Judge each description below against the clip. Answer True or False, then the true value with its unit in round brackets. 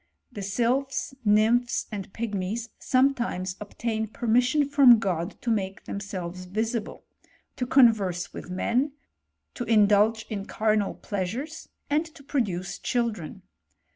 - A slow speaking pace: True (120 wpm)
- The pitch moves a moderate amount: True (3.9 semitones)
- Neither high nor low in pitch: False (220 Hz)